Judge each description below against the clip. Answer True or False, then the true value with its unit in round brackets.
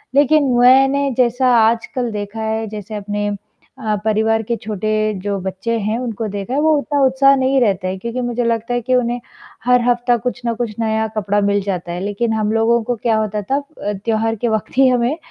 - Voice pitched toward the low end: False (225 Hz)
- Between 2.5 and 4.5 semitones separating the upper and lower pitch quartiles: True (2.8 semitones)